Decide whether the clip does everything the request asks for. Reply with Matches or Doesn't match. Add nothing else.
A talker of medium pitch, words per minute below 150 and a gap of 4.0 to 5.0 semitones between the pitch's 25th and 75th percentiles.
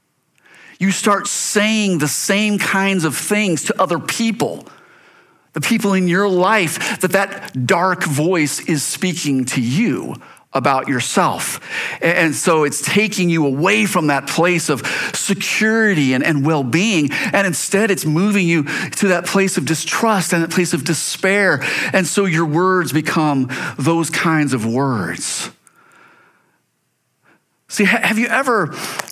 Matches